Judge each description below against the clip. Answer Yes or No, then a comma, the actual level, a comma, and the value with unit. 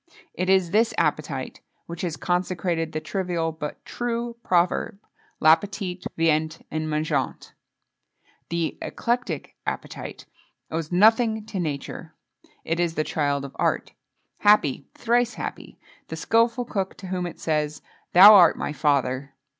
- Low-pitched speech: No, medium, 170 Hz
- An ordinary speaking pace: No, slow, 130 wpm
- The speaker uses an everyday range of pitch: Yes, average, 4.5 semitones